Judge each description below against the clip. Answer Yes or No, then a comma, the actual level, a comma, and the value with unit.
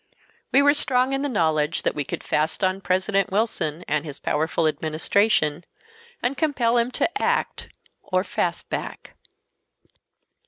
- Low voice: No, high, 190 Hz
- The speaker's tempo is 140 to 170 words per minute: Yes, average, 145 wpm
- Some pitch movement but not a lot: No, wide, 7.7 semitones